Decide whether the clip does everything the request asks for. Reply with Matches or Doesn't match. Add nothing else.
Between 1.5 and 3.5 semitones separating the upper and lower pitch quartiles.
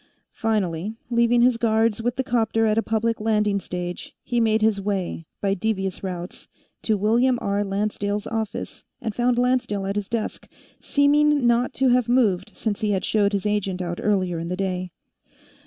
Matches